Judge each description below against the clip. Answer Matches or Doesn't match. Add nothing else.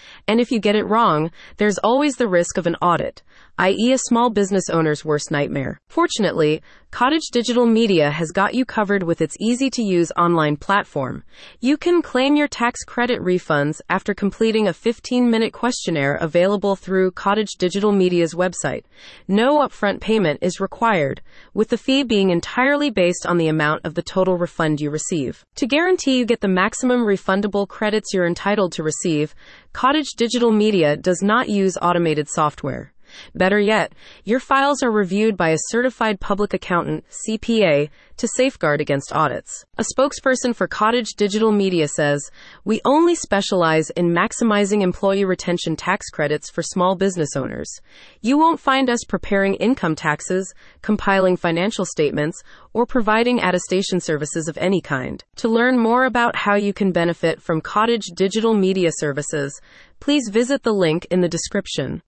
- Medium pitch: Doesn't match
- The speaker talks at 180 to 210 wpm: Doesn't match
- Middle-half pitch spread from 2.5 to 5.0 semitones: Doesn't match